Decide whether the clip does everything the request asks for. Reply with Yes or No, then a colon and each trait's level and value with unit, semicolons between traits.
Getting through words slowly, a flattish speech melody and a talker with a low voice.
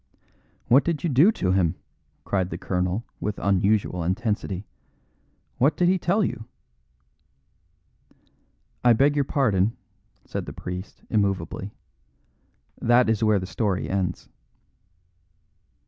No: slow, 115 wpm; wide, 5.4 semitones; low, 105 Hz